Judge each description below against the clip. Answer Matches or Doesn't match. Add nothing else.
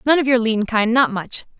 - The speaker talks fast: Matches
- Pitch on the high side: Matches